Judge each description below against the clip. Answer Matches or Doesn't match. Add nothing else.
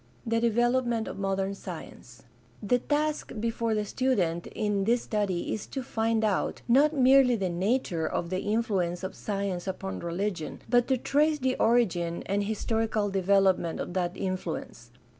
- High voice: Matches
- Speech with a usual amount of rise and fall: Matches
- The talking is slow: Doesn't match